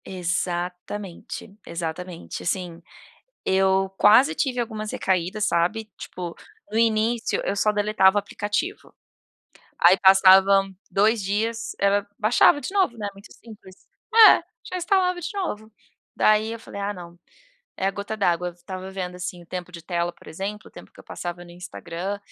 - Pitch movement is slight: No, average, 3.3 semitones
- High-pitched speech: Yes, high, 195 Hz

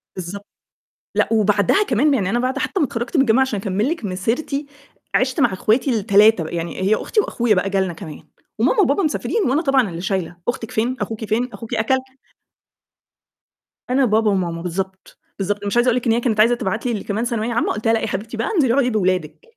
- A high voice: Yes, high, 220 Hz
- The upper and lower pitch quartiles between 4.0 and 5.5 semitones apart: Yes, average, 4.3 semitones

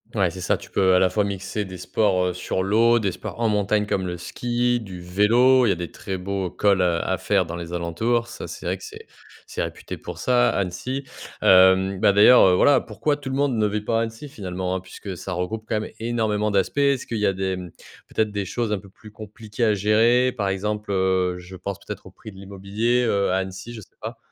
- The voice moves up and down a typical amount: Yes, average, 3.5 semitones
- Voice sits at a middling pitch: No, low, 100 Hz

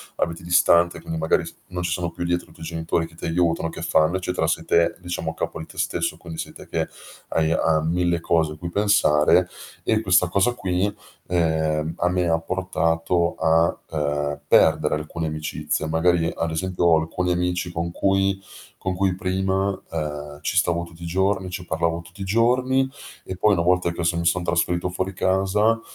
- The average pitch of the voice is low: Yes, very low, 85 Hz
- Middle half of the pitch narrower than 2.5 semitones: Yes, narrow, 2.1 semitones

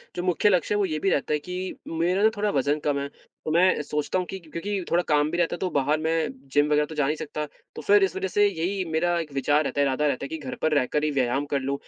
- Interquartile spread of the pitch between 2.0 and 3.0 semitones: No, average, 3.7 semitones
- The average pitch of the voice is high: No, medium, 155 Hz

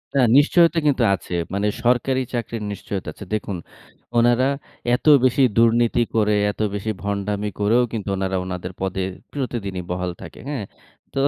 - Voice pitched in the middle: No, low, 110 Hz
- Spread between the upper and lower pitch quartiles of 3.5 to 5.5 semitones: Yes, average, 3.8 semitones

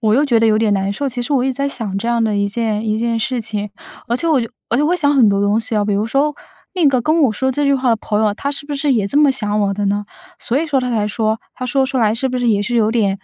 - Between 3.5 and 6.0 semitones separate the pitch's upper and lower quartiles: Yes, average, 4.2 semitones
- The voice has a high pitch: Yes, high, 230 Hz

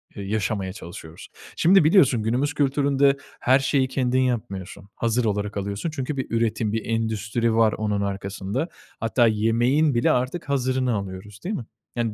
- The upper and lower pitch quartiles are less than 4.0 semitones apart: No, average, 4.3 semitones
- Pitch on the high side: No, low, 115 Hz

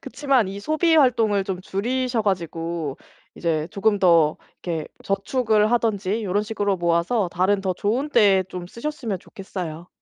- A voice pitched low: No, high, 200 Hz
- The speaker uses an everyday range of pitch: Yes, average, 4.3 semitones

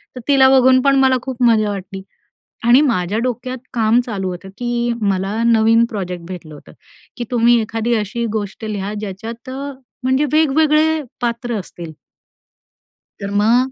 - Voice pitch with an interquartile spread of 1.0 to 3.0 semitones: No, average, 4.2 semitones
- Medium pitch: No, high, 235 Hz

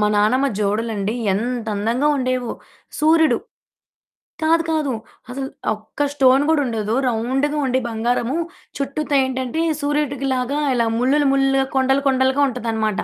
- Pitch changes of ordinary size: Yes, average, 3.4 semitones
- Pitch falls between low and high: No, very high, 260 Hz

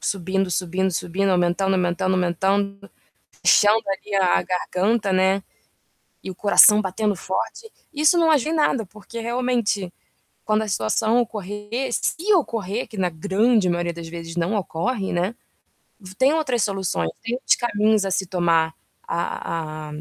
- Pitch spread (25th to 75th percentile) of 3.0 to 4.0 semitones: Yes, average, 3.7 semitones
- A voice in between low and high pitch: No, high, 195 Hz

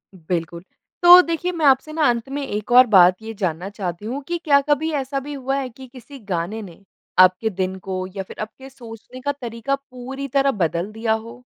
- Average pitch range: No, wide, 6.0 semitones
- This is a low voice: No, high, 240 Hz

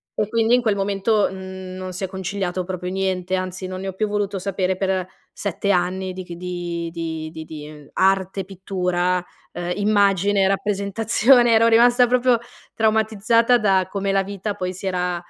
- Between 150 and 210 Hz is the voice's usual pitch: Yes, high, 190 Hz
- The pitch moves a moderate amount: No, narrow, 2.1 semitones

